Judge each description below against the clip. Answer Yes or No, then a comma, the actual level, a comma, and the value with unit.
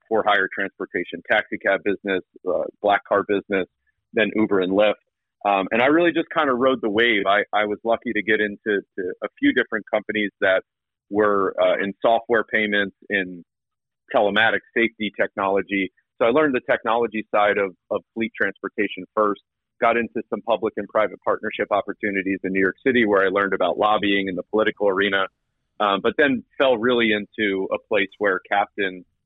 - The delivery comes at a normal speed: Yes, average, 180 wpm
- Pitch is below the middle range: Yes, low, 105 Hz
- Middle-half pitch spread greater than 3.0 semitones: No, narrow, 2.4 semitones